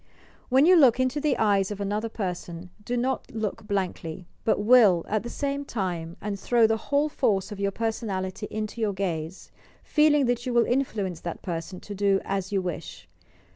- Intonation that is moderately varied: Yes, average, 4.4 semitones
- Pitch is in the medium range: No, high, 210 Hz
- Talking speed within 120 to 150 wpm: No, average, 185 wpm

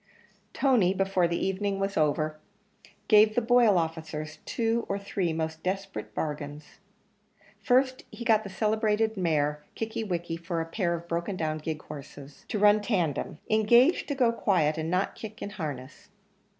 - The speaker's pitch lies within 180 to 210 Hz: Yes, medium, 185 Hz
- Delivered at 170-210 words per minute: No, average, 160 wpm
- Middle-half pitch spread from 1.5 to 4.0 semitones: No, average, 5.2 semitones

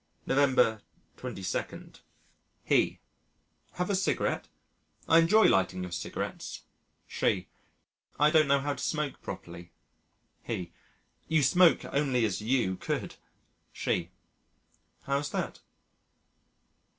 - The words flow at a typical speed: No, slow, 100 wpm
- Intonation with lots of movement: Yes, wide, 6.3 semitones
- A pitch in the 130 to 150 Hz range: Yes, medium, 140 Hz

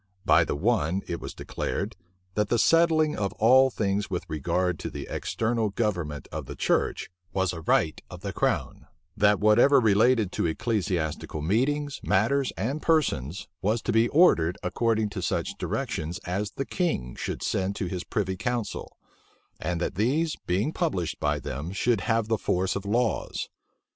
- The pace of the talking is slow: No, average, 165 wpm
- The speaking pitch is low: Yes, low, 105 Hz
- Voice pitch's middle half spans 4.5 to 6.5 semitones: Yes, average, 5.1 semitones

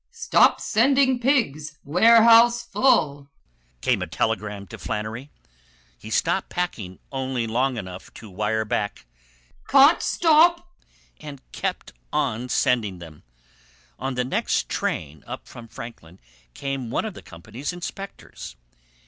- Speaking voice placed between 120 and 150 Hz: Yes, low, 135 Hz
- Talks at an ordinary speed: No, slow, 125 wpm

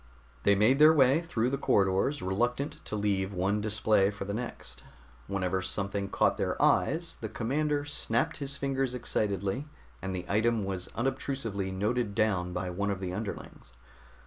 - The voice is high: No, low, 105 Hz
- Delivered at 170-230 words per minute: No, average, 160 wpm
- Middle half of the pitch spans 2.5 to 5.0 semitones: No, wide, 5.4 semitones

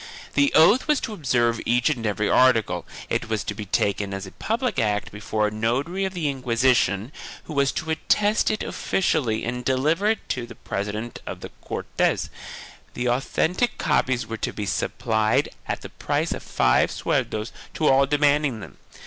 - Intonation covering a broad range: Yes, wide, 6.2 semitones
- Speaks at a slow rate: No, average, 180 wpm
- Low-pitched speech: Yes, low, 125 Hz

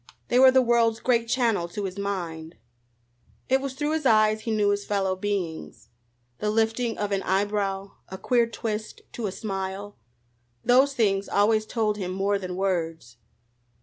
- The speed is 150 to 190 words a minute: Yes, average, 165 wpm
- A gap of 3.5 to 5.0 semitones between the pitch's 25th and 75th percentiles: No, average, 3.1 semitones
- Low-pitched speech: No, high, 205 Hz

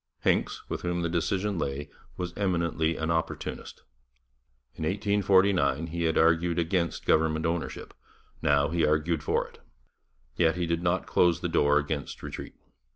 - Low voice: Yes, very low, 85 Hz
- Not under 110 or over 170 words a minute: Yes, average, 150 wpm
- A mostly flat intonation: Yes, narrow, 1.9 semitones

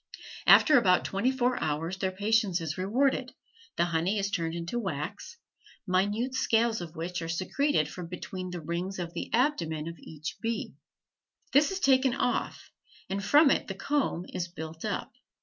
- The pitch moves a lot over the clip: Yes, wide, 6.1 semitones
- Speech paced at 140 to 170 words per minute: Yes, average, 165 wpm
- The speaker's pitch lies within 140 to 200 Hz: Yes, high, 190 Hz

